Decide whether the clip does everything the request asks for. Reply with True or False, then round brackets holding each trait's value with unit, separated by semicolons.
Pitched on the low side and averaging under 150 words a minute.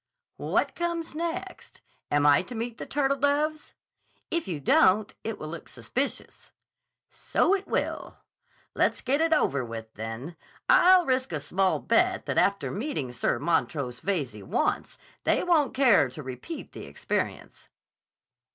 False (215 Hz; 140 wpm)